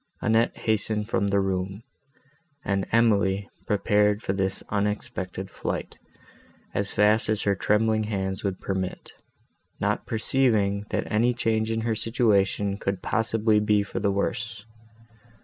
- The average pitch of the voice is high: No, low, 105 Hz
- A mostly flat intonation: Yes, narrow, 2.0 semitones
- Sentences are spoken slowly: Yes, slow, 130 wpm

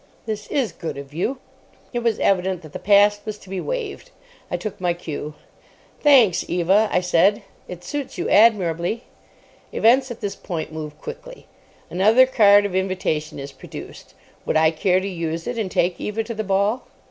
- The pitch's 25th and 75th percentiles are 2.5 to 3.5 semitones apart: No, average, 4.6 semitones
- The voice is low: No, high, 195 Hz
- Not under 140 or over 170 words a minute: No, average, 180 wpm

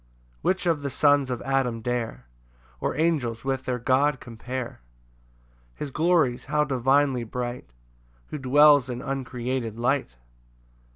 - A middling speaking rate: No, slow, 130 wpm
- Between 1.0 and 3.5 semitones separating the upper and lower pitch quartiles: Yes, average, 2.9 semitones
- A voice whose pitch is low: Yes, low, 130 Hz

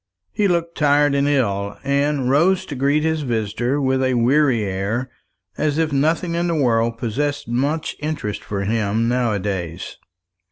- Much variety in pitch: No, average, 4.7 semitones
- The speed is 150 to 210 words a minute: Yes, average, 165 wpm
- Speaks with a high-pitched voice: No, low, 135 Hz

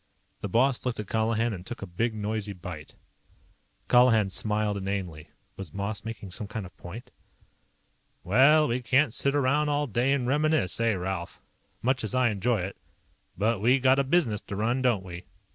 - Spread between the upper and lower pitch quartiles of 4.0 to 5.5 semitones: Yes, average, 4.5 semitones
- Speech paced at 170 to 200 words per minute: Yes, average, 180 wpm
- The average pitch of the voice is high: No, low, 110 Hz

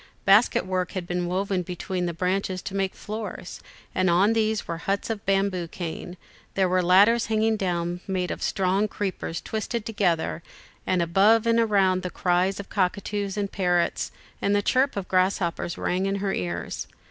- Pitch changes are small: Yes, narrow, 2.3 semitones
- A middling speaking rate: Yes, average, 170 wpm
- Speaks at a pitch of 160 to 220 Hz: Yes, high, 190 Hz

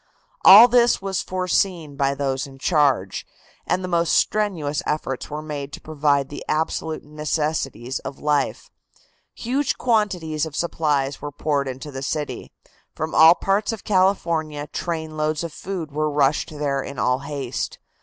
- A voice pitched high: No, medium, 155 Hz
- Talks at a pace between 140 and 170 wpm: Yes, average, 150 wpm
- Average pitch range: Yes, average, 3.5 semitones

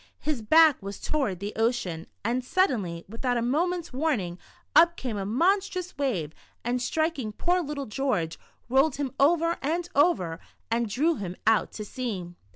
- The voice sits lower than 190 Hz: No, very high, 255 Hz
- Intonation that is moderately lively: No, wide, 7.3 semitones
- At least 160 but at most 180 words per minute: Yes, average, 170 wpm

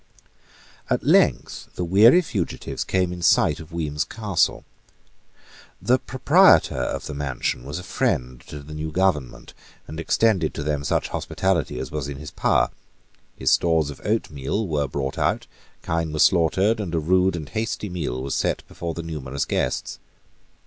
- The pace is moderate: Yes, average, 165 wpm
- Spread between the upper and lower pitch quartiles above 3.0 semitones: Yes, average, 4.6 semitones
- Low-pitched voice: Yes, very low, 80 Hz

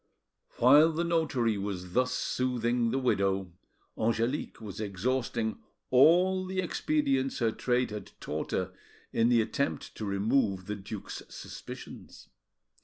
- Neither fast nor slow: No, slow, 125 wpm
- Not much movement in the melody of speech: No, average, 4.4 semitones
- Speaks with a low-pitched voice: Yes, low, 120 Hz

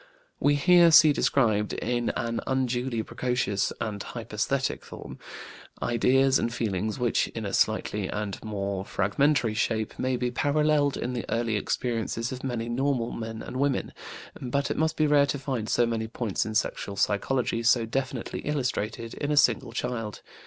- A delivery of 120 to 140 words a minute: No, average, 160 wpm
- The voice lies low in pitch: Yes, low, 120 Hz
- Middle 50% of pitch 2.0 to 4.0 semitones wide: Yes, average, 3.5 semitones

